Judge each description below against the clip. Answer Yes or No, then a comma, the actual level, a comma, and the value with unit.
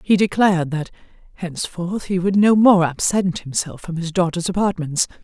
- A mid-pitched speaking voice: Yes, medium, 180 Hz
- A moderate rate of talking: Yes, average, 160 wpm